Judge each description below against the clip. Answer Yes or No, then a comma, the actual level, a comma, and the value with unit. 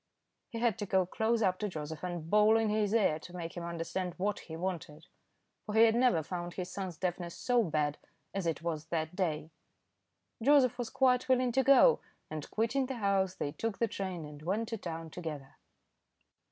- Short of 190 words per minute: No, average, 195 wpm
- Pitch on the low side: No, medium, 185 Hz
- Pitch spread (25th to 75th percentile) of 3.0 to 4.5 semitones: No, average, 5.3 semitones